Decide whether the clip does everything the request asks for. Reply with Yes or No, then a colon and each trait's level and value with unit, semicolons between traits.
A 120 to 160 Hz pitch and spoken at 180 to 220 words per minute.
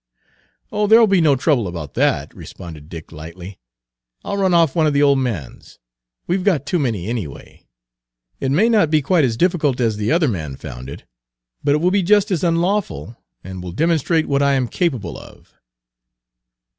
Yes: medium, 140 Hz; average, 185 wpm